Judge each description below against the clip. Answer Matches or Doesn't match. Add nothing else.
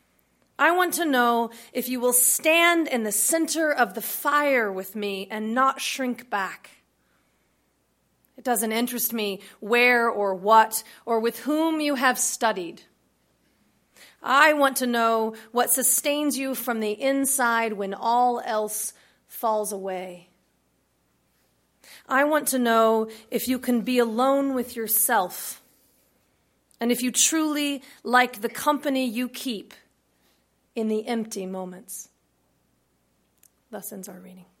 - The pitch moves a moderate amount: Matches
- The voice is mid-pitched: Doesn't match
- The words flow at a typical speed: Doesn't match